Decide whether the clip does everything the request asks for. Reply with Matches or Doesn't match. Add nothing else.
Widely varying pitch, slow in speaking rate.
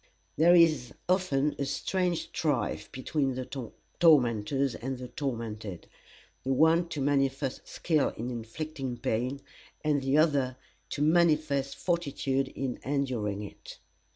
Doesn't match